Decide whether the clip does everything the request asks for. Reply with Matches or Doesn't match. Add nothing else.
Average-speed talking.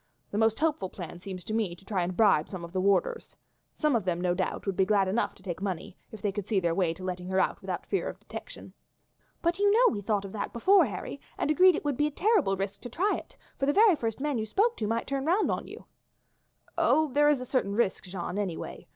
Doesn't match